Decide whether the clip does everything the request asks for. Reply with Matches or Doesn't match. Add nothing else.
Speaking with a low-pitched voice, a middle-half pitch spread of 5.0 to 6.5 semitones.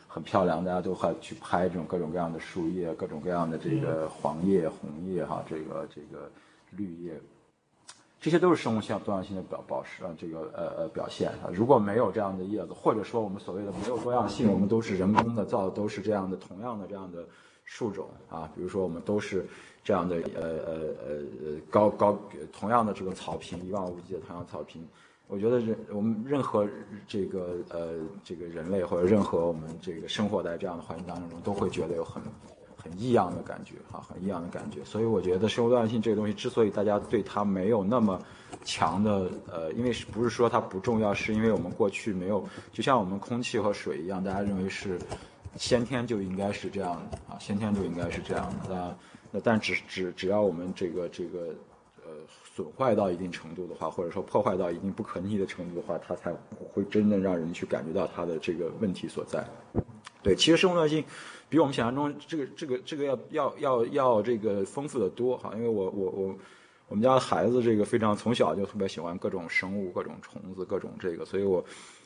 Doesn't match